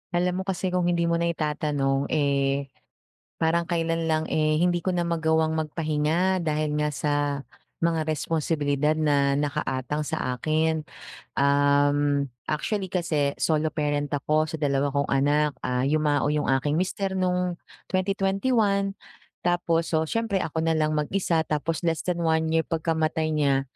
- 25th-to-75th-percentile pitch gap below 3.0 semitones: Yes, narrow, 2.6 semitones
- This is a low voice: No, medium, 155 Hz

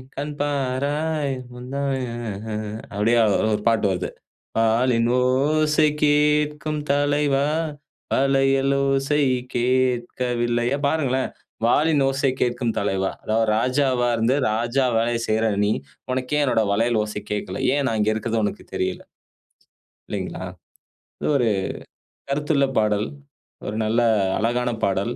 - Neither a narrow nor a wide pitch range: Yes, average, 3.7 semitones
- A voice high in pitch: No, low, 125 Hz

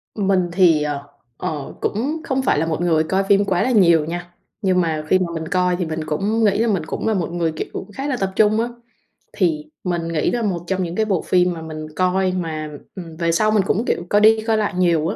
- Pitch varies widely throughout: No, average, 3.9 semitones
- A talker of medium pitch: Yes, medium, 180 Hz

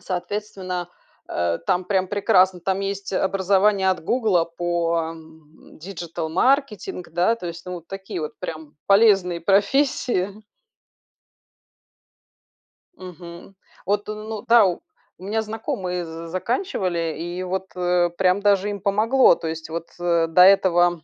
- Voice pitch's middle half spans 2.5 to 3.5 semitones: Yes, average, 2.8 semitones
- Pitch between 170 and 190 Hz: Yes, medium, 185 Hz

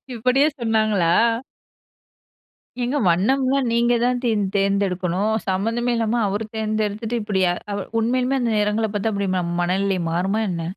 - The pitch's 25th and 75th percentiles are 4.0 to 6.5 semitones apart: No, average, 3.5 semitones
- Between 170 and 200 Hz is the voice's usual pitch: No, high, 215 Hz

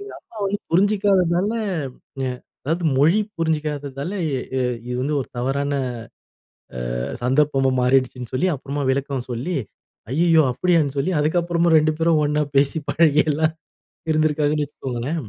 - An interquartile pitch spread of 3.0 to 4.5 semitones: Yes, average, 3.8 semitones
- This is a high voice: No, medium, 150 Hz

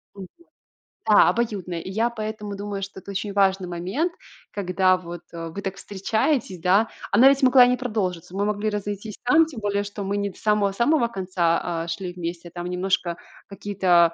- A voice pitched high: Yes, high, 200 Hz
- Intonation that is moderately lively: Yes, average, 3.0 semitones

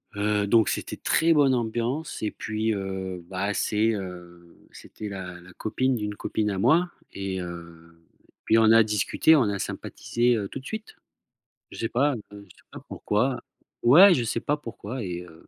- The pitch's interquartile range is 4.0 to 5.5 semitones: Yes, average, 4.3 semitones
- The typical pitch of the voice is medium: No, low, 105 Hz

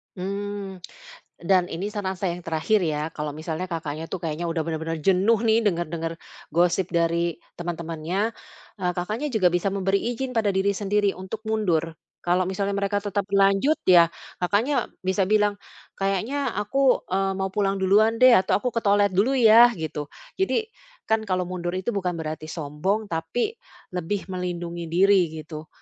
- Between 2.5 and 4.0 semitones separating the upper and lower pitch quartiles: Yes, average, 3.3 semitones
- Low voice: No, high, 190 Hz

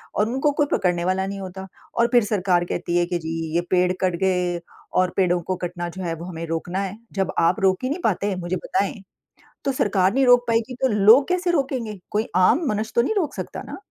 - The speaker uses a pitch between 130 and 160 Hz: No, high, 190 Hz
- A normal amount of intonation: Yes, average, 4.7 semitones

